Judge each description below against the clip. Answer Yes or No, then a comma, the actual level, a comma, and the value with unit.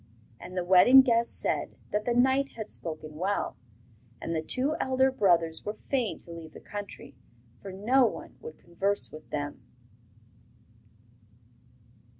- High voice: Yes, high, 205 Hz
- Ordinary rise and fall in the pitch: No, wide, 7.0 semitones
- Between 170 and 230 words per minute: No, average, 145 wpm